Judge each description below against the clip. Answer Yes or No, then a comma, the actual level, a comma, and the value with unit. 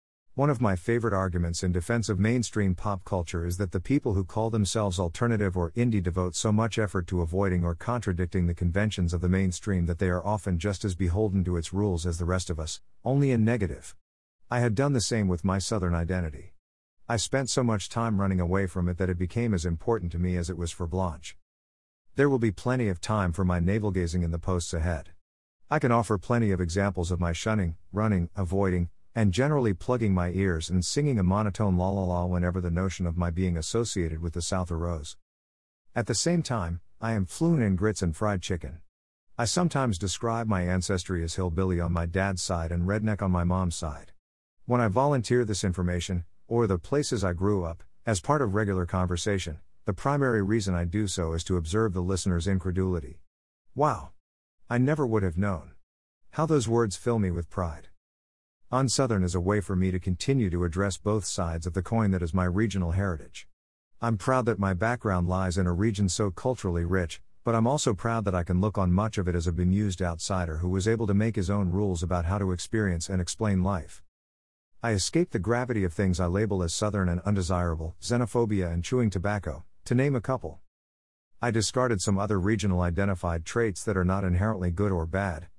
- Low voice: Yes, very low, 95 Hz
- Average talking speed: No, fast, 210 wpm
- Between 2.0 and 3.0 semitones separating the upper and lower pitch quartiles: No, average, 3.7 semitones